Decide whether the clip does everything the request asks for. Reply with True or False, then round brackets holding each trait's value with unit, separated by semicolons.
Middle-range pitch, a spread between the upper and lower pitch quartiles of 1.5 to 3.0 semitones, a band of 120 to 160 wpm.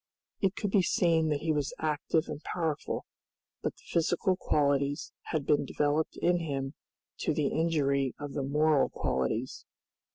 True (150 Hz; 2.7 semitones; 155 wpm)